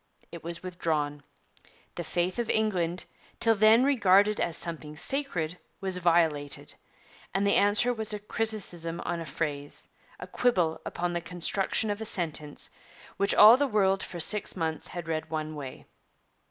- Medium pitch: Yes, medium, 180 Hz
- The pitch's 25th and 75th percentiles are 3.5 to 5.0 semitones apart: Yes, average, 4.4 semitones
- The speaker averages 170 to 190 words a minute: No, average, 155 wpm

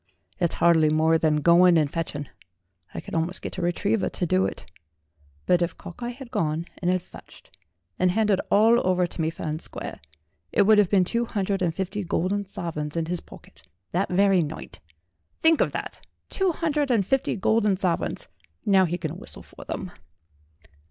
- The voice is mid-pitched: Yes, medium, 180 Hz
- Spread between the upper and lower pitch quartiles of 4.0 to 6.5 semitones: No, average, 3.6 semitones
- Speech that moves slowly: No, average, 185 wpm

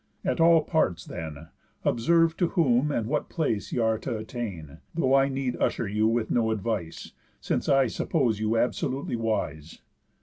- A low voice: Yes, low, 115 Hz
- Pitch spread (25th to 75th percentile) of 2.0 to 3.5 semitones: No, average, 4.3 semitones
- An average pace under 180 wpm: Yes, average, 165 wpm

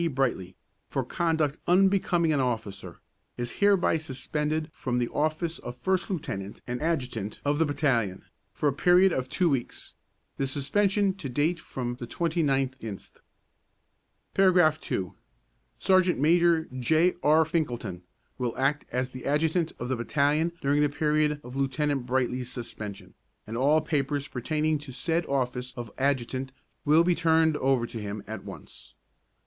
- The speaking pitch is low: No, medium, 145 Hz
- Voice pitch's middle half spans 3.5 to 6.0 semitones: Yes, average, 4.5 semitones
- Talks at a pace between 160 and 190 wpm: No, average, 145 wpm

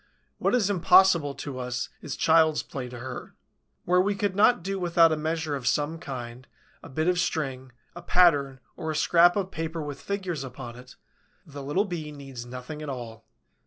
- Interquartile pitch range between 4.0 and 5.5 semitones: Yes, average, 4.9 semitones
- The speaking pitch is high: No, medium, 155 Hz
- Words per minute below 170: No, average, 190 wpm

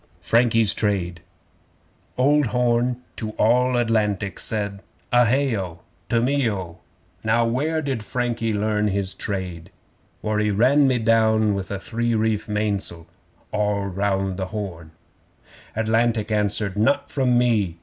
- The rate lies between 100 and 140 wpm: Yes, slow, 135 wpm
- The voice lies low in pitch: Yes, low, 110 Hz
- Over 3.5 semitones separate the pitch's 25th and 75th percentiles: No, average, 3.0 semitones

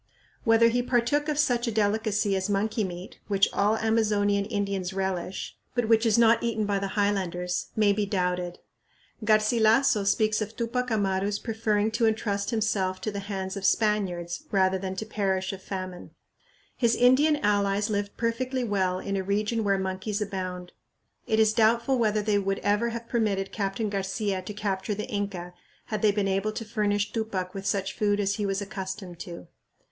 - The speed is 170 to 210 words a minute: Yes, average, 180 wpm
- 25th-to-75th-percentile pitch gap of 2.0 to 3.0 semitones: Yes, narrow, 2.4 semitones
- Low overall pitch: No, high, 205 Hz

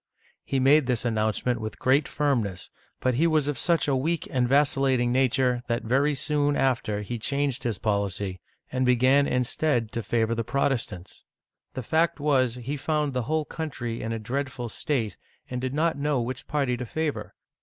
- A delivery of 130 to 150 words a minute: No, average, 185 wpm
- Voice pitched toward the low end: Yes, low, 130 Hz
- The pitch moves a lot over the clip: No, average, 3.5 semitones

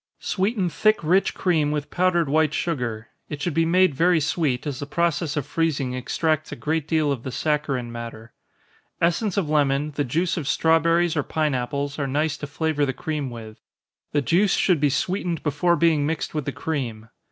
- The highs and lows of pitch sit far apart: No, average, 3.2 semitones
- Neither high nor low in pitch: Yes, medium, 150 Hz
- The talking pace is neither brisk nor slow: Yes, average, 195 wpm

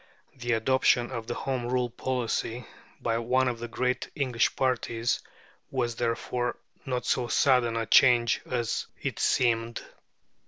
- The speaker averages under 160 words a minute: Yes, slow, 135 wpm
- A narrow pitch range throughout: Yes, narrow, 1.5 semitones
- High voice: No, low, 120 Hz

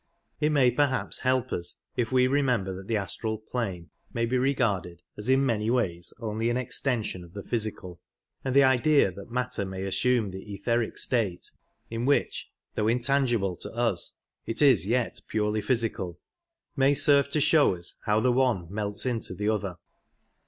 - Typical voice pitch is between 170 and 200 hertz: No, low, 115 Hz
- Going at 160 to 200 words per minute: Yes, average, 170 wpm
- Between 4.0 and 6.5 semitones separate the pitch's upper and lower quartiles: Yes, average, 4.4 semitones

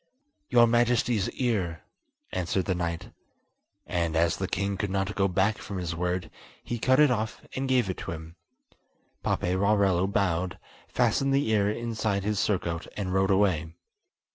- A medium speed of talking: Yes, average, 155 wpm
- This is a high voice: No, low, 100 Hz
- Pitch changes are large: No, average, 3.6 semitones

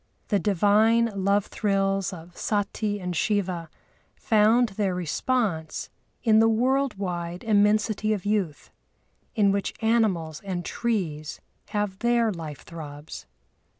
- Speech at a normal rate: No, slow, 115 wpm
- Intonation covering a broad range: No, average, 3.7 semitones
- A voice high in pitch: Yes, high, 200 Hz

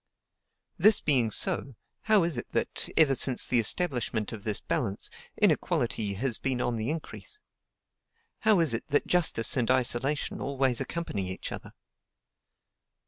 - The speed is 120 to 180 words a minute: Yes, average, 140 wpm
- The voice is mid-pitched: No, low, 130 Hz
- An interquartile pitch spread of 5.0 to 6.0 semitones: Yes, wide, 5.5 semitones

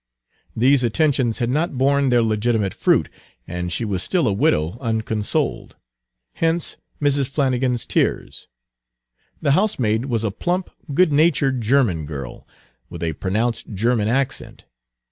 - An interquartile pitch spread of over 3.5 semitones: Yes, average, 4.7 semitones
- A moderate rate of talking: No, slow, 130 wpm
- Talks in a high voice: No, low, 120 Hz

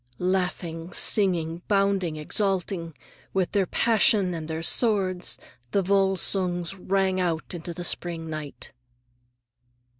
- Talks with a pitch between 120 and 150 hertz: No, medium, 180 Hz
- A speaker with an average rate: No, slow, 100 wpm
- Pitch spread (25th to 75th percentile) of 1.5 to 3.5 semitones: Yes, average, 2.8 semitones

